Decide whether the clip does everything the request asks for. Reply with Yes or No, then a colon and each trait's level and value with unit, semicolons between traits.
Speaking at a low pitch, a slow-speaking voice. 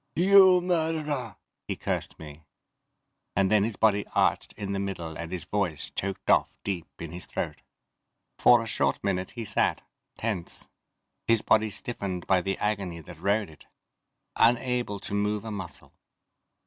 No: low, 100 Hz; average, 155 wpm